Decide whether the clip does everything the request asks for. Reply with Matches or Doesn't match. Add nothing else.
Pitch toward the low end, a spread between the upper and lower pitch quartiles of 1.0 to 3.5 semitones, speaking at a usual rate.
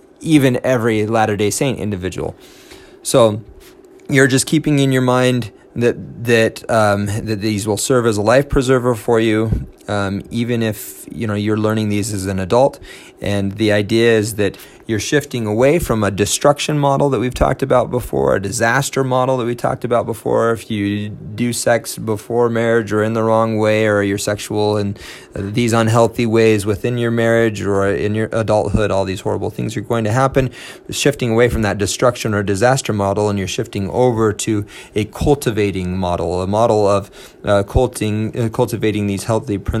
Matches